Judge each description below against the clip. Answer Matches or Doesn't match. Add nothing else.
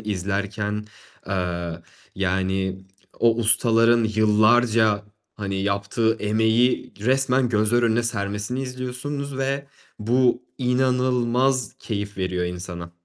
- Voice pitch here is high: Doesn't match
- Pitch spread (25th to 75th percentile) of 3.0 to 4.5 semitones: Matches